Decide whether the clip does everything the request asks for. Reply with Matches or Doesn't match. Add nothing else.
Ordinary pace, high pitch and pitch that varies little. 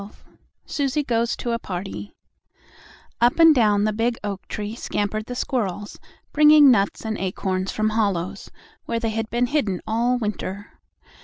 Doesn't match